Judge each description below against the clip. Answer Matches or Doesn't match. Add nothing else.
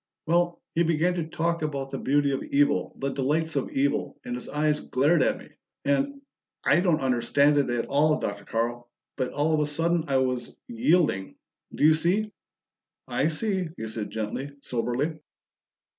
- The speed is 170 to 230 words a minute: Matches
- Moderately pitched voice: Matches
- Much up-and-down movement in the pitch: Doesn't match